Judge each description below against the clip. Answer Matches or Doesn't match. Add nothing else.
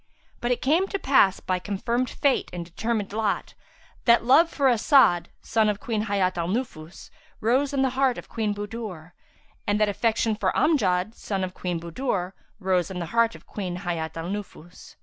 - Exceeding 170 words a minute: Matches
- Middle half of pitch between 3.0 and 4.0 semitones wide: Doesn't match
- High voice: Matches